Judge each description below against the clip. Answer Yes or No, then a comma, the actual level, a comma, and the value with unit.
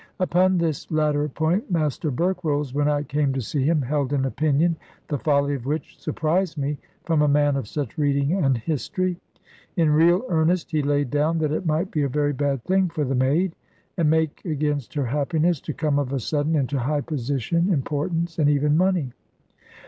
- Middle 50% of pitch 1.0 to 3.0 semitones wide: Yes, narrow, 2.5 semitones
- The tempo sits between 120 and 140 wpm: No, average, 190 wpm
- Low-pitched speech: No, medium, 150 Hz